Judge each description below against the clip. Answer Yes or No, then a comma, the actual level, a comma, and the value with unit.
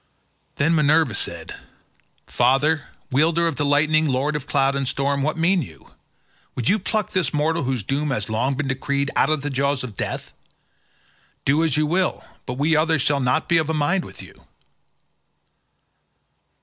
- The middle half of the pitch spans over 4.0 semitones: No, average, 2.9 semitones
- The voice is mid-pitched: Yes, medium, 145 Hz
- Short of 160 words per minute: No, average, 175 wpm